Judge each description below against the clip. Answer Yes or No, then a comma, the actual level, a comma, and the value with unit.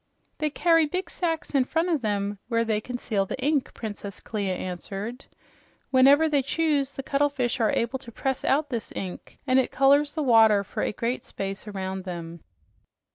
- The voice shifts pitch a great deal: Yes, wide, 5.7 semitones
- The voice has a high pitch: Yes, very high, 250 Hz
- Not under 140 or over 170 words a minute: No, average, 180 wpm